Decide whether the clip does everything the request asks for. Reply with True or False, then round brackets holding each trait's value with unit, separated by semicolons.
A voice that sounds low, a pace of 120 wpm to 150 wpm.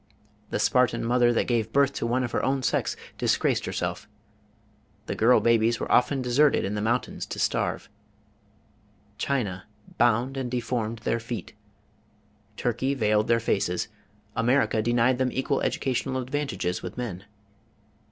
True (120 Hz; 140 wpm)